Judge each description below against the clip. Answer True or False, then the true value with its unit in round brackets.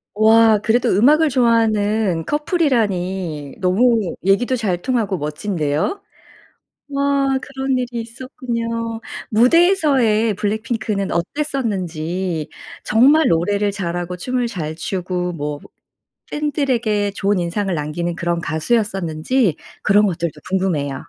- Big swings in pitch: True (5.7 semitones)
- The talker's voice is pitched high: True (210 Hz)